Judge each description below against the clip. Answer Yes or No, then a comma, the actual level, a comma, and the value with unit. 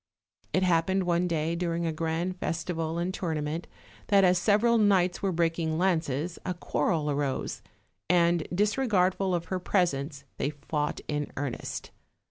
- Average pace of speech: Yes, average, 145 wpm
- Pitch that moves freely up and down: No, narrow, 2.6 semitones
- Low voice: No, medium, 170 Hz